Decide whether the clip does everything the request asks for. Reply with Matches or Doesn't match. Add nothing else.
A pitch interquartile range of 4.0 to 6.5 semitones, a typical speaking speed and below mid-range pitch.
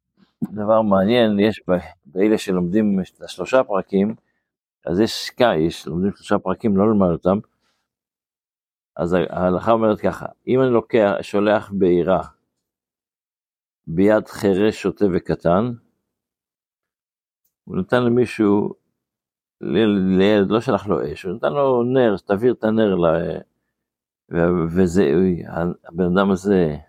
Doesn't match